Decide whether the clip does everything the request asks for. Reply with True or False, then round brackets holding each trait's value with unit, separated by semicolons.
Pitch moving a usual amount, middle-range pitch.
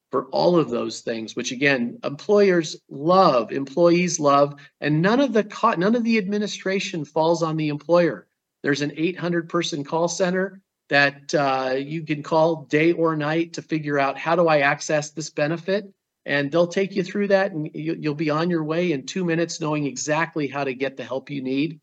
True (3.3 semitones; 160 Hz)